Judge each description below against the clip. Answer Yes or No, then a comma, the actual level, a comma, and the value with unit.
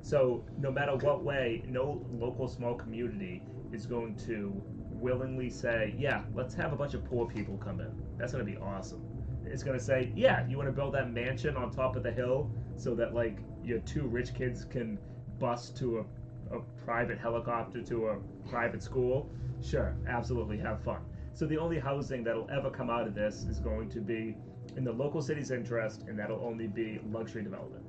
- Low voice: Yes, low, 120 Hz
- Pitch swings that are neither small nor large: No, narrow, 2.2 semitones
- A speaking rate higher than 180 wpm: Yes, average, 200 wpm